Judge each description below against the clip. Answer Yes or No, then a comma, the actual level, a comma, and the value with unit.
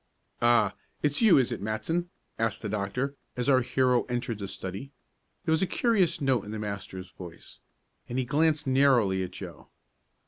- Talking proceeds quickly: No, average, 175 wpm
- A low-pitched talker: Yes, low, 125 Hz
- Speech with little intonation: No, wide, 5.4 semitones